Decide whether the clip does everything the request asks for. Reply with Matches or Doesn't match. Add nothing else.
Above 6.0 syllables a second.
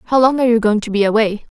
Matches